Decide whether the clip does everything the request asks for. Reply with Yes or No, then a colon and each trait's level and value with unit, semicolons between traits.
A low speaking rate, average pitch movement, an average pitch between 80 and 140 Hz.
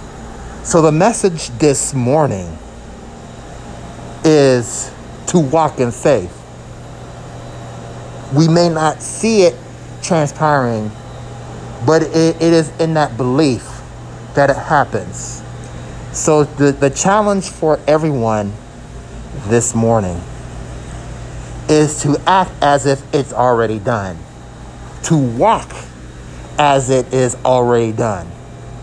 Yes: slow, 100 wpm; average, 4.9 semitones; low, 135 Hz